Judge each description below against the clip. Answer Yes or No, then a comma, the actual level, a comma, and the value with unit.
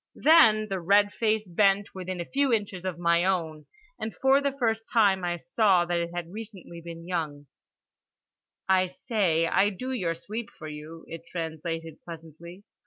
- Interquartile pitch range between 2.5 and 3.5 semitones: No, average, 4.1 semitones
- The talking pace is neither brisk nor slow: Yes, average, 165 wpm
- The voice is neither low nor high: Yes, medium, 180 Hz